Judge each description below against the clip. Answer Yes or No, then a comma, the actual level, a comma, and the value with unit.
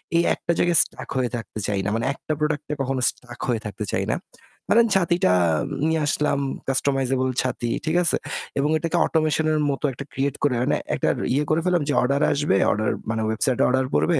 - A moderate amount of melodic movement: Yes, average, 3.8 semitones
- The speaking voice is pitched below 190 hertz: Yes, medium, 140 Hz